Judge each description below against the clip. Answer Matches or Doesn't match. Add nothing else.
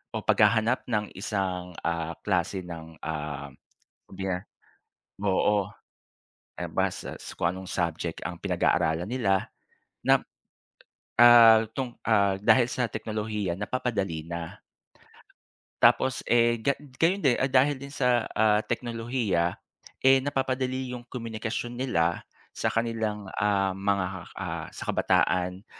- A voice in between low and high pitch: Doesn't match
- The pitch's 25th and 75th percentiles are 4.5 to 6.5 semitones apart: Matches